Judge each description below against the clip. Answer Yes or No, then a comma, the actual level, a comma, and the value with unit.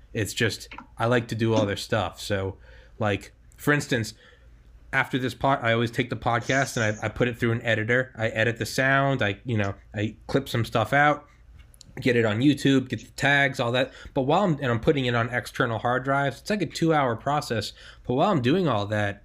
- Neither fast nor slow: No, fast, 230 wpm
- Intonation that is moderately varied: Yes, average, 3.7 semitones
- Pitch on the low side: Yes, low, 120 Hz